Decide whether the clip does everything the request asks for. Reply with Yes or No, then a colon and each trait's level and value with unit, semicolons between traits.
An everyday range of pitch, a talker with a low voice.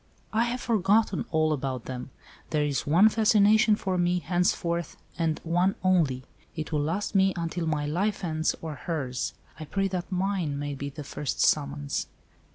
No: average, 4.6 semitones; medium, 170 Hz